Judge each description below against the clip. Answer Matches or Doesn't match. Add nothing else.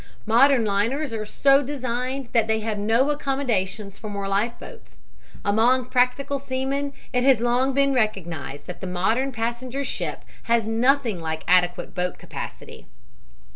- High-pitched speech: Matches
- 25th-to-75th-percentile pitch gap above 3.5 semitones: Matches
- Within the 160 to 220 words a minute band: Doesn't match